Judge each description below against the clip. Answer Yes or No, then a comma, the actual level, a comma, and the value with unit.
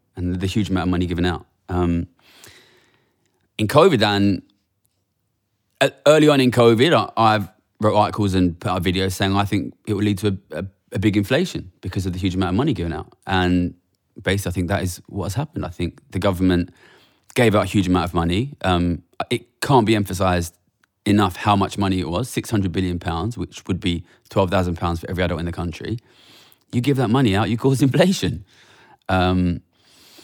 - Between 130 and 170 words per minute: No, average, 190 wpm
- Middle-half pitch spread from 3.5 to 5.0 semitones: No, average, 3.0 semitones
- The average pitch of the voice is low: Yes, very low, 95 Hz